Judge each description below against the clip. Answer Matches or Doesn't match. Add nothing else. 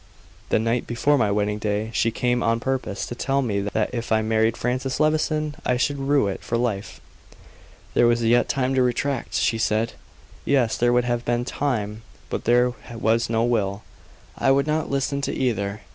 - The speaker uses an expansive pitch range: Doesn't match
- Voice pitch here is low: Matches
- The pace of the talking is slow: Doesn't match